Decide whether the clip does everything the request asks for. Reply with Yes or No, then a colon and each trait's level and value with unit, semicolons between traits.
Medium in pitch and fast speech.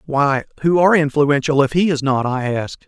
Yes: medium, 145 Hz; fast, 210 wpm